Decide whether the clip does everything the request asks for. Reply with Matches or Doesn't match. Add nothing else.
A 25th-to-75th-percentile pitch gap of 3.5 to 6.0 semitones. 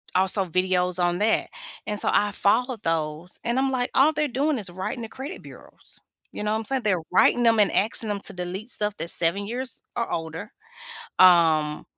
Matches